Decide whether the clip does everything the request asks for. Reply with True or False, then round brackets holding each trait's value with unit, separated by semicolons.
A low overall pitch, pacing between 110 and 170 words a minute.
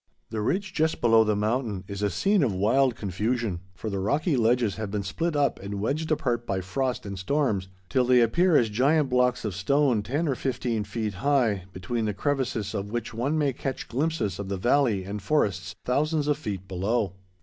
False (115 Hz; 200 wpm)